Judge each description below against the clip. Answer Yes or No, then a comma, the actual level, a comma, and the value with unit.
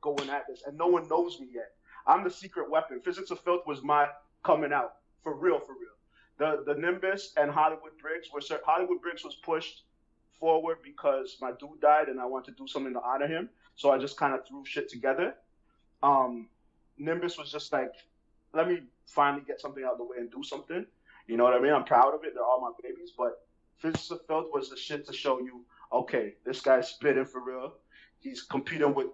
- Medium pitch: Yes, medium, 155 Hz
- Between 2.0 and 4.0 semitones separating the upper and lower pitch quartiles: No, average, 4.5 semitones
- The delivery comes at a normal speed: No, fast, 220 wpm